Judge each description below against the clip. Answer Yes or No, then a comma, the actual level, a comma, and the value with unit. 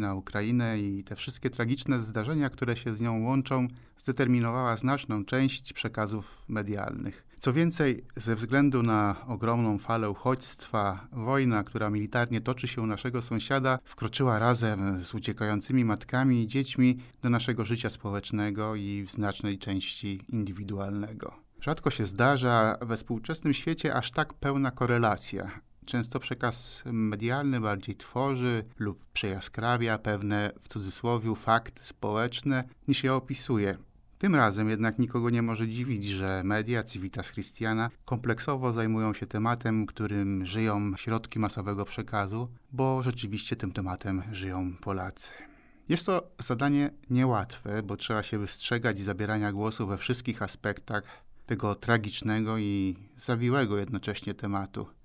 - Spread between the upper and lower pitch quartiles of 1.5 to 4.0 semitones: Yes, average, 3.4 semitones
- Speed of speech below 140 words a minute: Yes, average, 130 wpm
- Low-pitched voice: Yes, low, 115 Hz